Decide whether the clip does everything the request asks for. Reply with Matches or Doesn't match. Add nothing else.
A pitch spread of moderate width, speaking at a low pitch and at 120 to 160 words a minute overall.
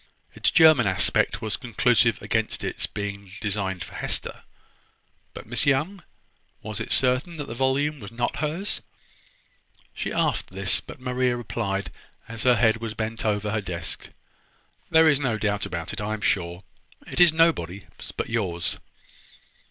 Matches